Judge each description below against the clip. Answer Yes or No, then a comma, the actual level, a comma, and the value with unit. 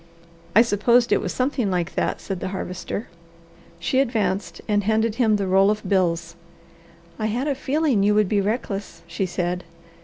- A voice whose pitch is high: Yes, high, 205 Hz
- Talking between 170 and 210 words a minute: Yes, average, 175 wpm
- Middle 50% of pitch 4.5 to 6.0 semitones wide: No, average, 3.7 semitones